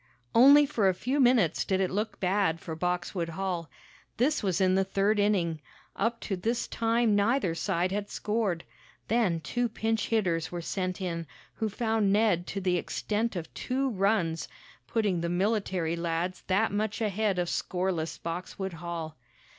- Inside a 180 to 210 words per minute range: No, average, 160 wpm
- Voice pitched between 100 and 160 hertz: No, high, 195 Hz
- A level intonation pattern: No, average, 4.0 semitones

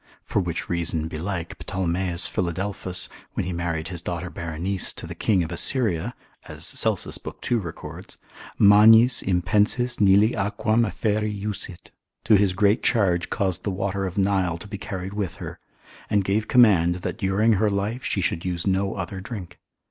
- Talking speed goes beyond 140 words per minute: Yes, average, 165 wpm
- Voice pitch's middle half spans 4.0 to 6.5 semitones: No, average, 3.0 semitones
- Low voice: Yes, very low, 95 Hz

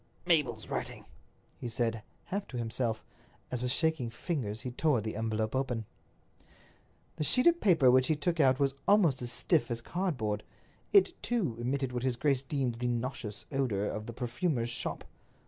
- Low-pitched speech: Yes, low, 125 Hz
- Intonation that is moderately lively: Yes, average, 4.3 semitones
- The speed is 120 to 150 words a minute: No, average, 170 wpm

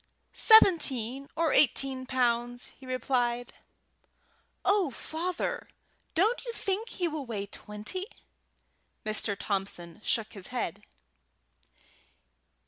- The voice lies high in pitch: Yes, very high, 255 Hz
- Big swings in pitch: Yes, wide, 6.8 semitones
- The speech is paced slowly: Yes, slow, 95 wpm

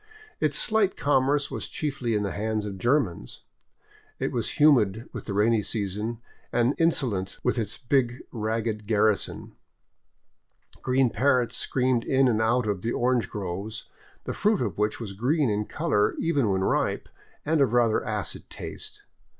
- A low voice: Yes, low, 115 Hz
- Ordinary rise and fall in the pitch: Yes, average, 4.0 semitones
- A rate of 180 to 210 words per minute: No, average, 155 wpm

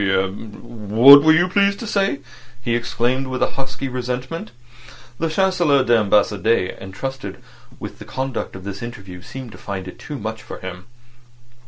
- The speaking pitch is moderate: No, low, 120 Hz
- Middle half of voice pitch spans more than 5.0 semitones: Yes, wide, 5.5 semitones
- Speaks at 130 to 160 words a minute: Yes, average, 155 wpm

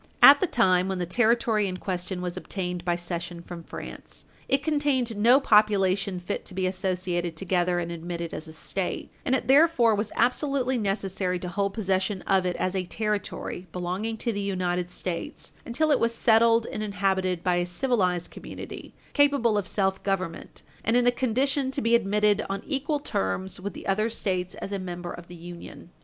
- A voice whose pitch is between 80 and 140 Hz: No, high, 195 Hz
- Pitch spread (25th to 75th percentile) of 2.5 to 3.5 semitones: No, average, 4.4 semitones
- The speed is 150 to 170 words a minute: No, average, 185 wpm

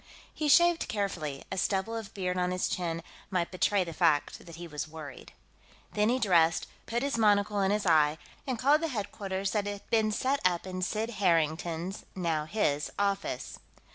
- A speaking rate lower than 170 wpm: No, average, 180 wpm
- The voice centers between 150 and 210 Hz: Yes, high, 190 Hz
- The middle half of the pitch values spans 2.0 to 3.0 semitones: No, average, 4.2 semitones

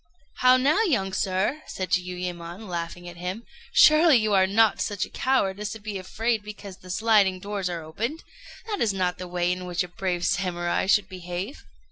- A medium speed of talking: Yes, average, 190 wpm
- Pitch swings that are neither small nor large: Yes, average, 3.6 semitones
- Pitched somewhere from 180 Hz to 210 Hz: Yes, high, 190 Hz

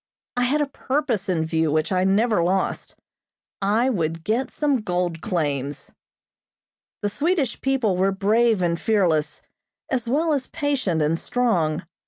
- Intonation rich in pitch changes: Yes, wide, 7.0 semitones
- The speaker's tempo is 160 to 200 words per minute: No, average, 145 wpm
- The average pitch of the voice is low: No, high, 200 Hz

